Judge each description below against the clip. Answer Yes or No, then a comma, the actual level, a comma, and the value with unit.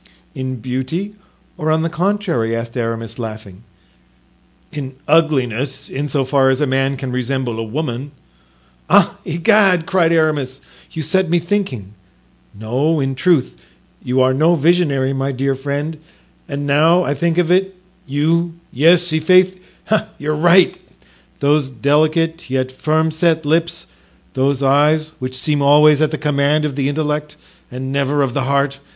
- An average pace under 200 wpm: Yes, average, 145 wpm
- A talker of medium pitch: Yes, medium, 145 Hz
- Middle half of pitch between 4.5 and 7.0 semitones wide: No, average, 3.6 semitones